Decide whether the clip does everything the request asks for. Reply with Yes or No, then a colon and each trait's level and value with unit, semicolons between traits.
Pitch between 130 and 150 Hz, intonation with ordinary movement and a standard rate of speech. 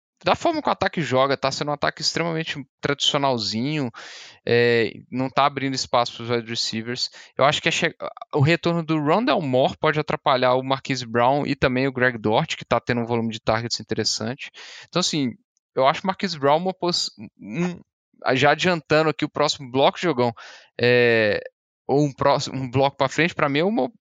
No: medium, 140 Hz; average, 4.5 semitones; fast, 190 wpm